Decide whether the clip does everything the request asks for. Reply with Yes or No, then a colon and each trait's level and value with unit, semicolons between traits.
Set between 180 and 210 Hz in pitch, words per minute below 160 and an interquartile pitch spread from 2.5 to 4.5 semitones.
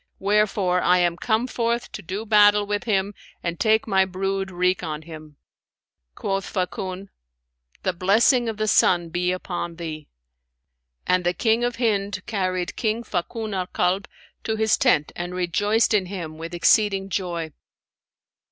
Yes: high, 190 Hz; average, 150 wpm; average, 3.2 semitones